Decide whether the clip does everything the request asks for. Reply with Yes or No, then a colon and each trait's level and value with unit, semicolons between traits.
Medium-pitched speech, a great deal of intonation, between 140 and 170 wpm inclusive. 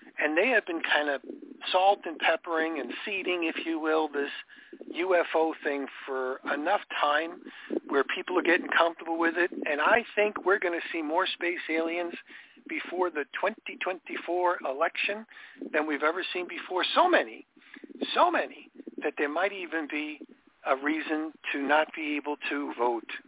Yes: medium, 170 Hz; wide, 7.4 semitones; average, 160 wpm